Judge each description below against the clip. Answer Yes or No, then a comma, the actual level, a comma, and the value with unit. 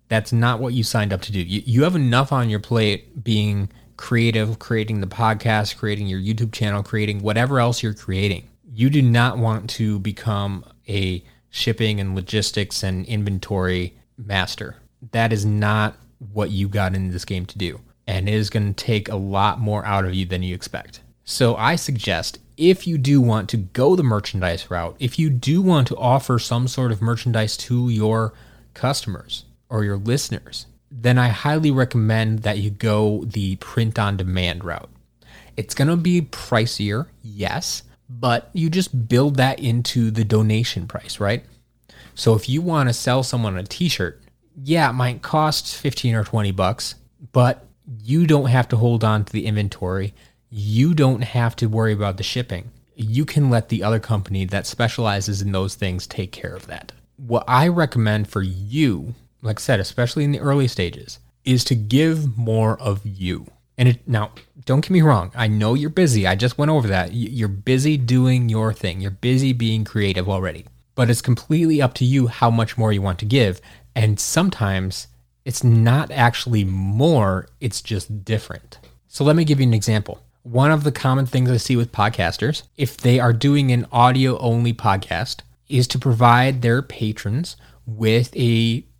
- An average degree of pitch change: Yes, average, 3.6 semitones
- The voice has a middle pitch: No, low, 115 Hz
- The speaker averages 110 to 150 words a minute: No, average, 185 wpm